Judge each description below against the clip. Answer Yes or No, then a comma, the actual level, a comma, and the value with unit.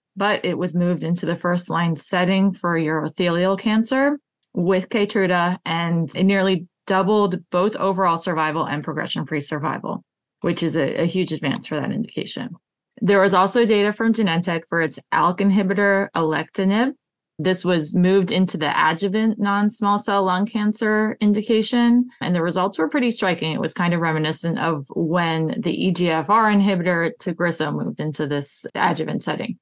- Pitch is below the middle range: No, medium, 185 Hz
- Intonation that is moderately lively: Yes, average, 3.4 semitones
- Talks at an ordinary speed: Yes, average, 160 wpm